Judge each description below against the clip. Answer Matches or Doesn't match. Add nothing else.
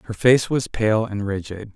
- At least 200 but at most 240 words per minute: Matches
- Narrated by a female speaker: Doesn't match